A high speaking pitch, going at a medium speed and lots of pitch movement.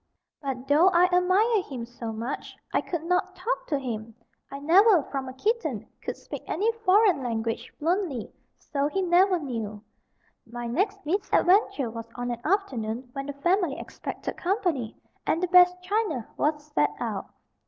Yes: very high, 310 Hz; average, 160 wpm; wide, 7.1 semitones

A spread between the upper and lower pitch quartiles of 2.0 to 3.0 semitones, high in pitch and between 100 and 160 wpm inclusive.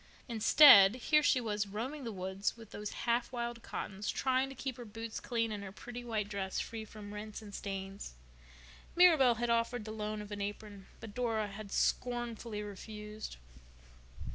No: narrow, 2.6 semitones; high, 220 Hz; average, 170 wpm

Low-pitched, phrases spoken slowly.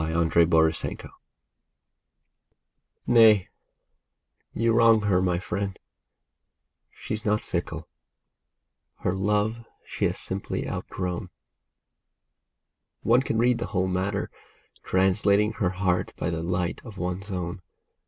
Yes: very low, 95 Hz; slow, 105 wpm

